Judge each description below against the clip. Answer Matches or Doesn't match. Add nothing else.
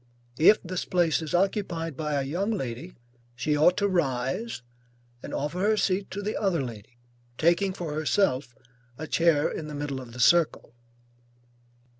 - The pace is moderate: Matches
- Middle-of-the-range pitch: Matches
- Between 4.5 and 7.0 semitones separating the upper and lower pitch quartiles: Matches